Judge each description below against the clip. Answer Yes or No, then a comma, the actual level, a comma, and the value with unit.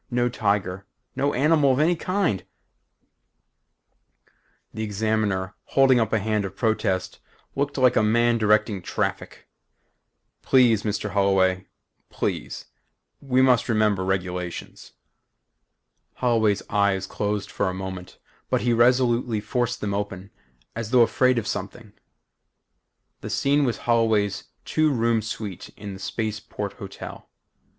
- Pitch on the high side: No, low, 110 Hz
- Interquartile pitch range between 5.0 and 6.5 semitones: No, average, 3.5 semitones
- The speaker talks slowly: Yes, slow, 125 wpm